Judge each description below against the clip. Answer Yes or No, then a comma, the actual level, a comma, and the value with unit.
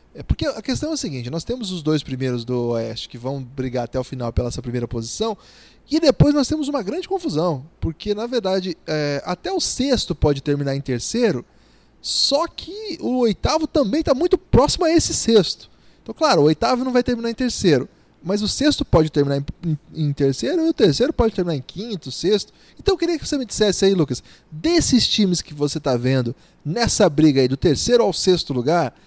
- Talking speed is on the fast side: Yes, fast, 210 wpm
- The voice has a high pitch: No, medium, 175 Hz